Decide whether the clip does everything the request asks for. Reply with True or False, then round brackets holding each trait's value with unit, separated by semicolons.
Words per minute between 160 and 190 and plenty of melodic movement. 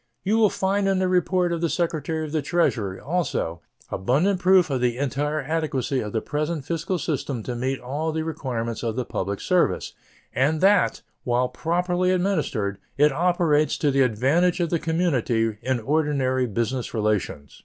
True (170 wpm; 5.7 semitones)